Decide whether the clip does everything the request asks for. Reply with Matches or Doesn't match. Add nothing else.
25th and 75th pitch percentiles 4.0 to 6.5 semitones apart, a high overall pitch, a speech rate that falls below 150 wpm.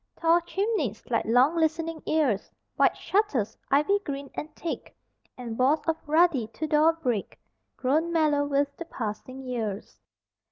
Matches